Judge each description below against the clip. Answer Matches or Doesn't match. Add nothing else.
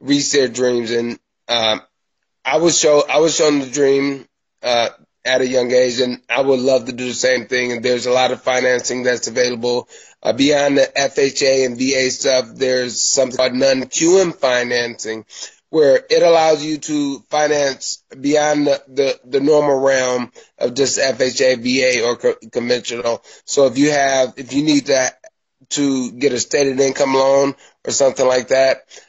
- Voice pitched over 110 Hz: Matches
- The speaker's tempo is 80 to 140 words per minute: Doesn't match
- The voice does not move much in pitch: Matches